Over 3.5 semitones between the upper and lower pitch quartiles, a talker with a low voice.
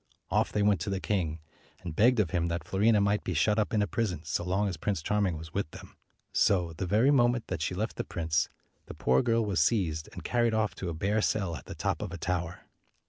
Yes: average, 4.0 semitones; very low, 95 Hz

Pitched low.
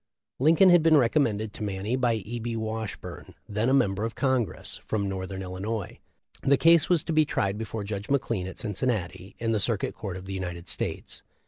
Yes: low, 110 Hz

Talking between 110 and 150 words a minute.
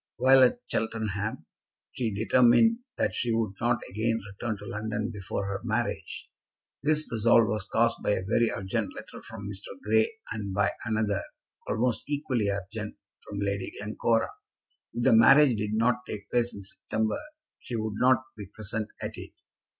No: average, 160 wpm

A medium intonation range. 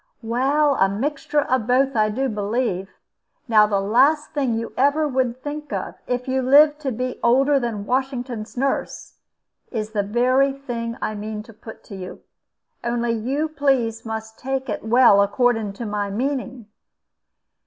Yes: average, 3.7 semitones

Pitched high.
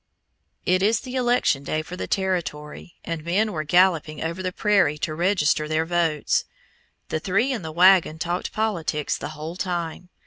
No: medium, 175 Hz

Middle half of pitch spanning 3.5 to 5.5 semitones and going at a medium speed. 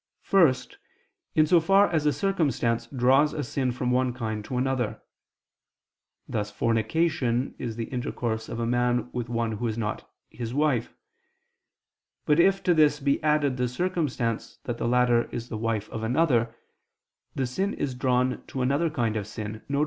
Yes: average, 4.1 semitones; average, 170 wpm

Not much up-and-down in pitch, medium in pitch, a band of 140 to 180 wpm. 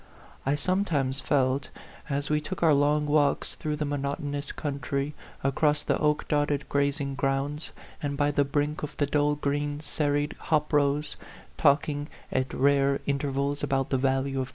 Yes: narrow, 1.2 semitones; medium, 145 Hz; average, 170 wpm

